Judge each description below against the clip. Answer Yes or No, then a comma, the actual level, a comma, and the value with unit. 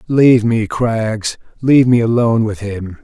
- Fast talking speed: No, average, 140 wpm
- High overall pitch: No, low, 115 Hz